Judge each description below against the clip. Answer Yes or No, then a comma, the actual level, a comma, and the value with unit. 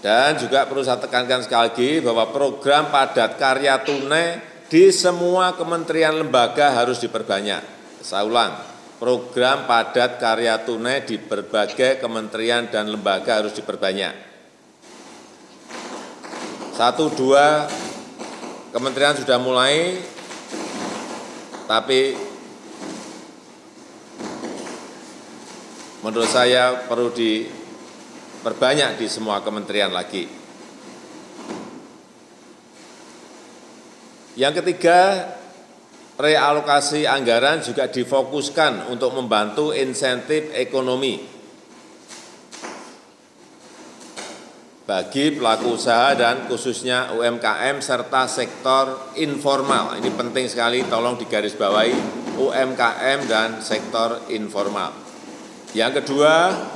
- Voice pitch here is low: Yes, low, 130 Hz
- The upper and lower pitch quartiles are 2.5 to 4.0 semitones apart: Yes, average, 3.6 semitones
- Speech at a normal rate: No, slow, 80 wpm